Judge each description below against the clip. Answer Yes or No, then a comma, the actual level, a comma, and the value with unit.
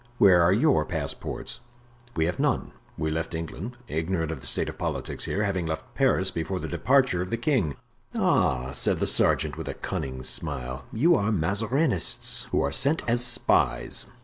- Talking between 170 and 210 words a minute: Yes, average, 175 wpm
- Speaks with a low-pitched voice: Yes, very low, 90 Hz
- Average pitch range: No, wide, 6.6 semitones